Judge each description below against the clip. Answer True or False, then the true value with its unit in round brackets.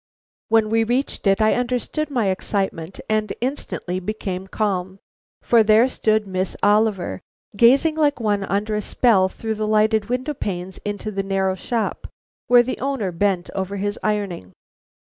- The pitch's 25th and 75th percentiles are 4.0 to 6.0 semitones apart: False (3.2 semitones)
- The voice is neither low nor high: False (210 Hz)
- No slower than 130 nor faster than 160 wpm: True (155 wpm)